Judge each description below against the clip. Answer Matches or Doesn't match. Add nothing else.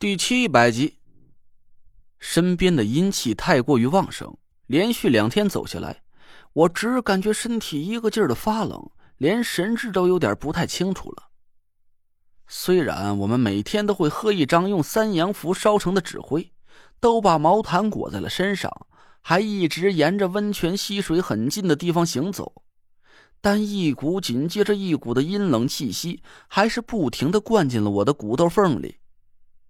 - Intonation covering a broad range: Matches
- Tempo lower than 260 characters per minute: Matches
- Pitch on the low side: Doesn't match